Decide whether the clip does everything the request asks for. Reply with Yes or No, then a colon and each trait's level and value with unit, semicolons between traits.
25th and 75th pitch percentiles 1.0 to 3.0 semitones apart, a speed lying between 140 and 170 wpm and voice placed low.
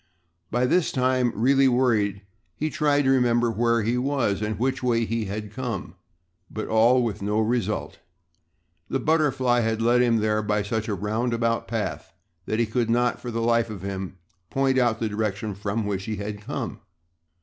No: average, 2.7 semitones; average, 180 wpm; low, 115 Hz